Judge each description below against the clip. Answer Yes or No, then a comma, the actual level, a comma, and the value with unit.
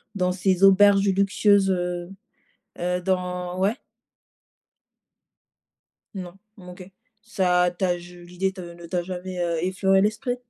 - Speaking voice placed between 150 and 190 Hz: Yes, medium, 185 Hz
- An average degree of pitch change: No, narrow, 1.5 semitones